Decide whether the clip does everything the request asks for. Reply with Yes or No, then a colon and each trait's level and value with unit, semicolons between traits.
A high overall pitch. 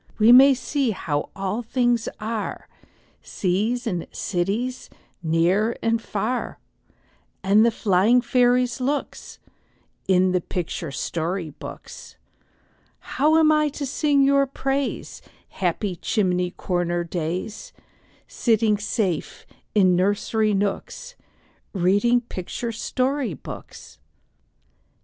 Yes: high, 215 Hz